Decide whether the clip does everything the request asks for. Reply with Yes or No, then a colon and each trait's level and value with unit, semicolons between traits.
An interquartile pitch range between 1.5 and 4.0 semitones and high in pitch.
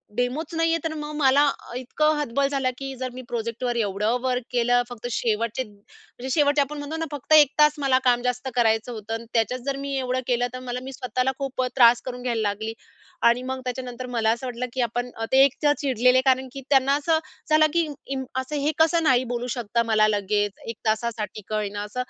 Yes: average, 2.9 semitones; very high, 250 Hz